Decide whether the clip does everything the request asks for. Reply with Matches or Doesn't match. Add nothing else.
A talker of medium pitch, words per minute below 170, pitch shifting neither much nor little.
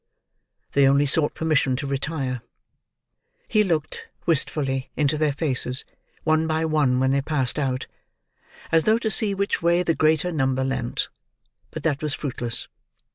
Matches